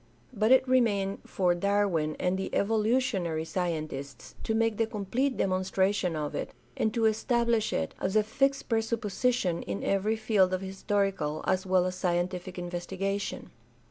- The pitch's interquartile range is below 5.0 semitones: Yes, average, 3.7 semitones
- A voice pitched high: Yes, high, 195 Hz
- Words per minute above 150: No, average, 145 wpm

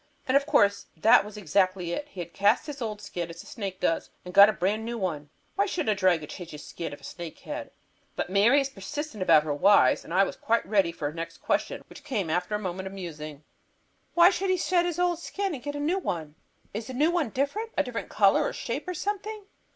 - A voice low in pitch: No, high, 210 Hz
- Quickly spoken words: Yes, fast, 250 wpm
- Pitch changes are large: Yes, wide, 8.6 semitones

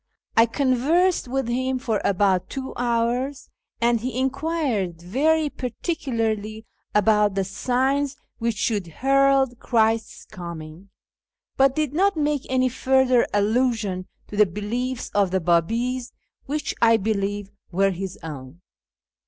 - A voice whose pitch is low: No, high, 235 Hz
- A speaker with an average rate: No, slow, 125 wpm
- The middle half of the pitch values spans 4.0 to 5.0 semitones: Yes, average, 4.6 semitones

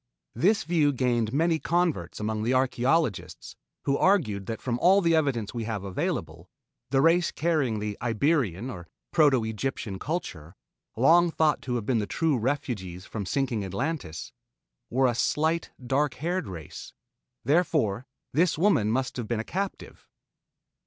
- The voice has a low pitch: Yes, low, 130 Hz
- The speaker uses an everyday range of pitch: No, wide, 6.7 semitones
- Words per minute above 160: No, average, 150 wpm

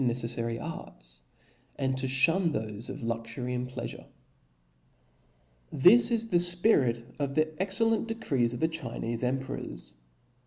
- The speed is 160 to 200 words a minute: No, average, 140 wpm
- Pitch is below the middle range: Yes, low, 130 Hz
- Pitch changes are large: Yes, wide, 6.9 semitones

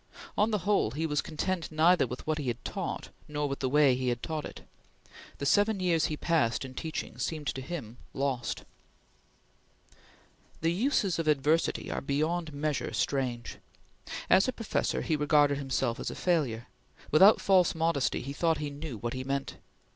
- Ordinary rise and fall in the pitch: Yes, average, 3.8 semitones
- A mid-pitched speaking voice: Yes, medium, 150 Hz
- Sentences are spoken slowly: No, average, 175 wpm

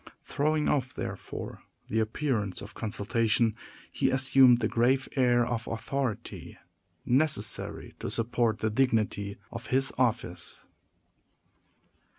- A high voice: No, low, 120 Hz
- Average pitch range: Yes, average, 3.1 semitones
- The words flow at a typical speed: No, slow, 110 wpm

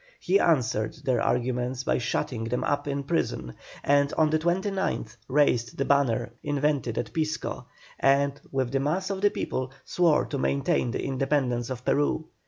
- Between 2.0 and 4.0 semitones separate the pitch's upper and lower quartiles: Yes, average, 3.5 semitones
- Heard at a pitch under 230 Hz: Yes, medium, 140 Hz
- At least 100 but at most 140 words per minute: No, average, 165 wpm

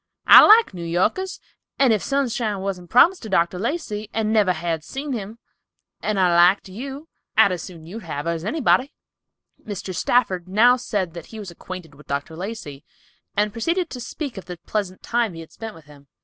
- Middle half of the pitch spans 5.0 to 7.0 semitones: Yes, wide, 5.5 semitones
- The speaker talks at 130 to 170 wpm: No, average, 195 wpm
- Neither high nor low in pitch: No, high, 200 Hz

